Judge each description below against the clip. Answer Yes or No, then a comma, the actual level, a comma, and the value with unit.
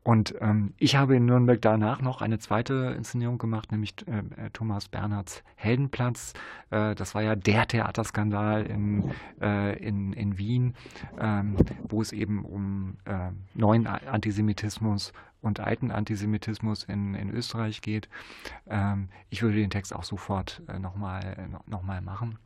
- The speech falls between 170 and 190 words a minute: No, average, 145 wpm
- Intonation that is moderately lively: No, narrow, 1.9 semitones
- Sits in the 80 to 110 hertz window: Yes, low, 105 Hz